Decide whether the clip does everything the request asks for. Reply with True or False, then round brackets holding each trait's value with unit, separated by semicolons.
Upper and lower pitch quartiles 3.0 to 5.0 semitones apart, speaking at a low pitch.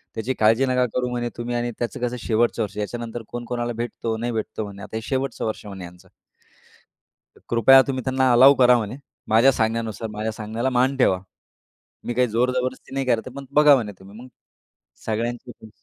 False (2.4 semitones; 120 Hz)